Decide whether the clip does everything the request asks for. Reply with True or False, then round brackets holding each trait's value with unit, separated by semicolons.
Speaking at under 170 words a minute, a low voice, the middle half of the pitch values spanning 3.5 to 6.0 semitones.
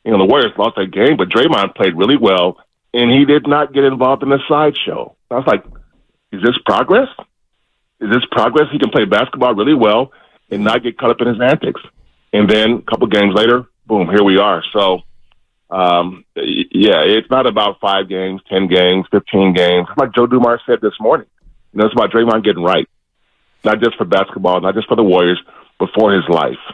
False (205 wpm; 110 Hz; 4.9 semitones)